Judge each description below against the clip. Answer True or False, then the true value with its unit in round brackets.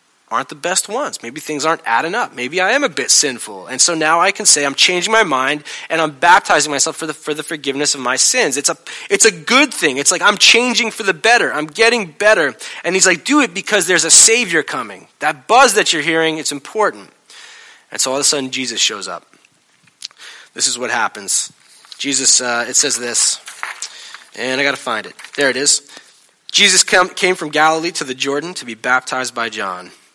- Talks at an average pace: False (215 wpm)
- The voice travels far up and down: True (6.6 semitones)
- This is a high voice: False (160 Hz)